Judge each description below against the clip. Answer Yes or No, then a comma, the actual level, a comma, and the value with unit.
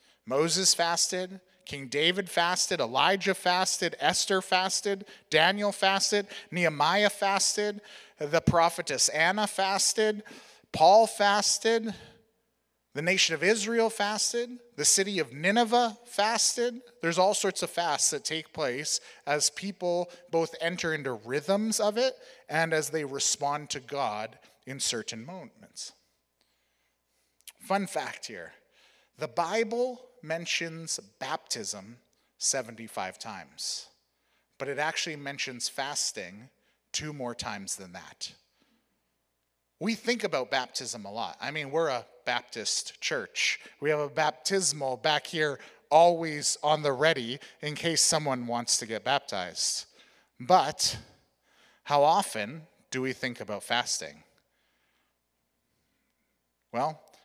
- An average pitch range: No, wide, 6.1 semitones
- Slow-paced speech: Yes, slow, 115 wpm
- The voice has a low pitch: No, medium, 170 Hz